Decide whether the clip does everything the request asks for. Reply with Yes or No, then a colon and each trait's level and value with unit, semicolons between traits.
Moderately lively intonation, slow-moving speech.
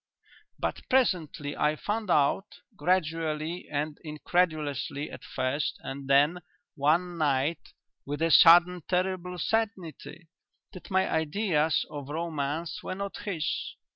Yes: average, 3.5 semitones; slow, 115 wpm